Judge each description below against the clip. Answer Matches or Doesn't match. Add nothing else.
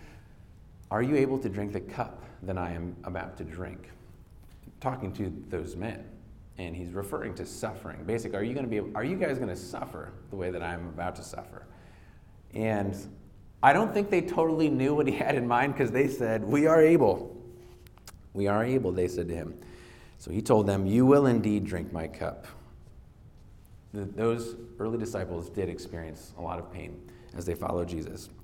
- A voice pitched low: Matches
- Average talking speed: Matches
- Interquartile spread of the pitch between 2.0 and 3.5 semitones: Doesn't match